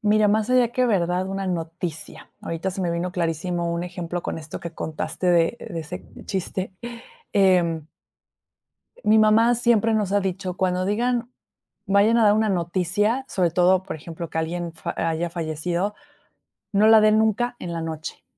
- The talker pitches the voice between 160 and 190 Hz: Yes, medium, 185 Hz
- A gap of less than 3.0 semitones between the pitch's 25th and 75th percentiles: No, average, 3.9 semitones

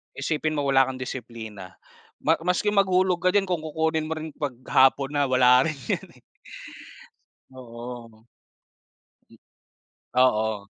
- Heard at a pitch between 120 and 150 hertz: Yes, low, 135 Hz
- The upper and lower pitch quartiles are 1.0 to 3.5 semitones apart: No, average, 4.8 semitones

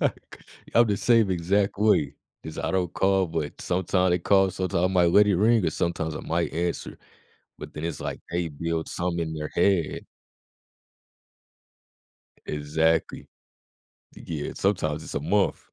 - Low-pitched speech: Yes, very low, 85 Hz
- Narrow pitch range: No, average, 3.1 semitones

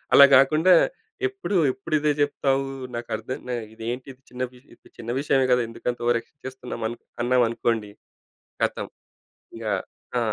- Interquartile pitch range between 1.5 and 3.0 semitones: Yes, average, 2.7 semitones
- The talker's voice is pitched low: Yes, low, 125 Hz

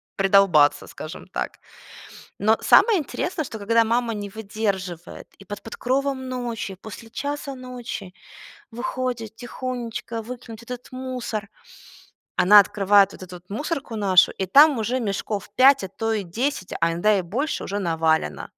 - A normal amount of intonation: Yes, average, 4.3 semitones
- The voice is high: Yes, high, 225 Hz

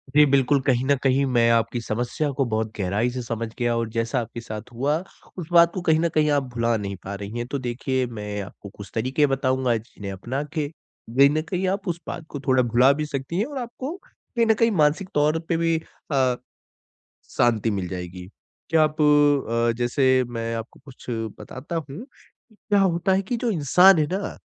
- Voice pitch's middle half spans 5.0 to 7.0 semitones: Yes, average, 5.3 semitones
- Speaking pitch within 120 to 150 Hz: Yes, low, 135 Hz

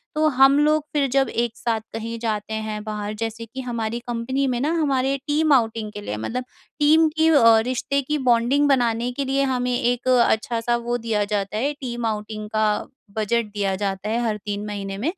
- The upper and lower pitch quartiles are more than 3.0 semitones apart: Yes, average, 3.8 semitones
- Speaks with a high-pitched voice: Yes, high, 235 Hz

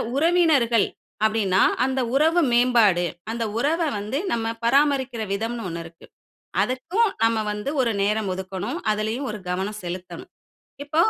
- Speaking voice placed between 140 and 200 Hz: No, high, 230 Hz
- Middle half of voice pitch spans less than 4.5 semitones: No, average, 4.9 semitones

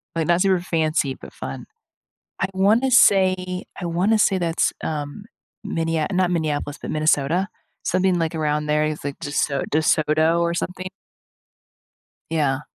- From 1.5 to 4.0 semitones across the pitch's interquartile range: Yes, average, 3.4 semitones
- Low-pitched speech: No, medium, 165 Hz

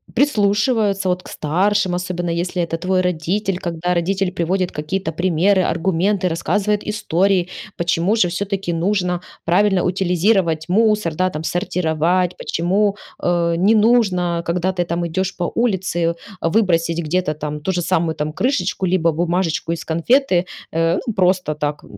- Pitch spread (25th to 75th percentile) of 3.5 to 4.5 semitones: No, narrow, 2.6 semitones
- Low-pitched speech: No, medium, 180 Hz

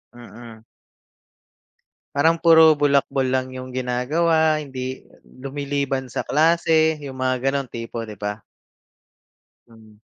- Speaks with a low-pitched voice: Yes, low, 130 Hz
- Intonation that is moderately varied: Yes, average, 3.3 semitones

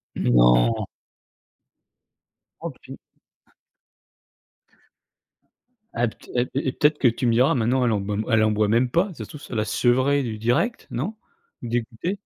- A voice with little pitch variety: No, average, 3.8 semitones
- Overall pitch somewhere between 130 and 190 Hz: No, low, 120 Hz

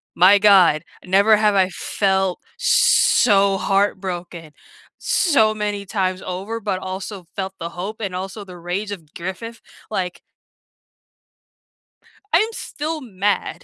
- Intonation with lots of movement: No, narrow, 2.5 semitones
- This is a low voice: No, high, 195 Hz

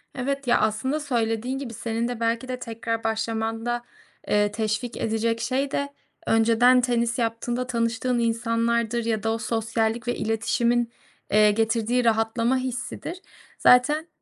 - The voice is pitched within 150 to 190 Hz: No, high, 230 Hz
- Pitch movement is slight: Yes, narrow, 1.8 semitones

